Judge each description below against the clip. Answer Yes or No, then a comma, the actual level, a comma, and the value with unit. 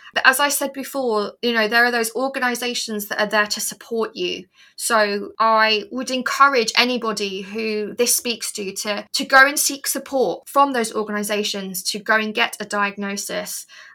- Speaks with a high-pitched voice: Yes, high, 225 Hz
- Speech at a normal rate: Yes, average, 175 wpm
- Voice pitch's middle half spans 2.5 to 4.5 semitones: Yes, average, 3.7 semitones